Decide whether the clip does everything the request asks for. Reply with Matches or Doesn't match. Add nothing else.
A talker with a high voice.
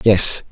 Doesn't match